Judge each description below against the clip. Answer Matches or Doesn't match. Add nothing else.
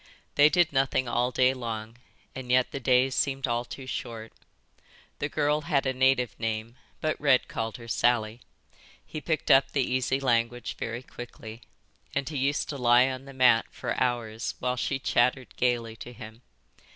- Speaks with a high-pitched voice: Doesn't match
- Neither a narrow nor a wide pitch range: Doesn't match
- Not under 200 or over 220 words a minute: Doesn't match